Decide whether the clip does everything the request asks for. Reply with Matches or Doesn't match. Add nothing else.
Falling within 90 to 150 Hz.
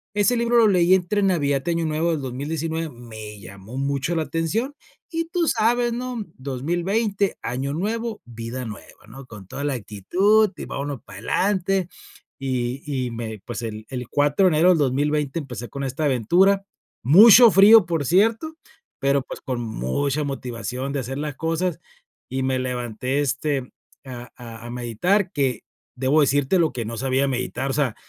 Matches